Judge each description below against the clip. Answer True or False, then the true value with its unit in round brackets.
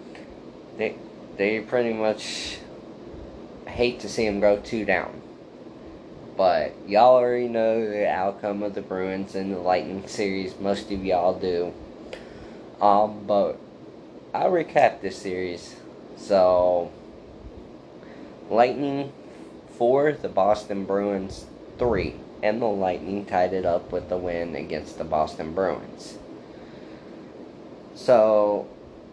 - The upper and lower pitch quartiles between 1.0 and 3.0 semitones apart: True (2.4 semitones)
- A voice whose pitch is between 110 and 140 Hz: False (100 Hz)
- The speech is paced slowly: True (115 wpm)